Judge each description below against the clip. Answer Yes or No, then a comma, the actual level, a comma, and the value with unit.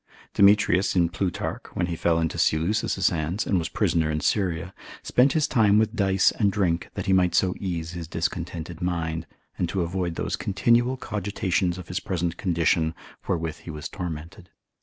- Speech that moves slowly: No, average, 170 wpm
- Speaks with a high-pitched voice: No, very low, 90 Hz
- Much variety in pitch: No, average, 2.9 semitones